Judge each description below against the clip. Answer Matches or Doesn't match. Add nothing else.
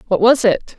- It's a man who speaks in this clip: Doesn't match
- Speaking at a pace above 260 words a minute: Doesn't match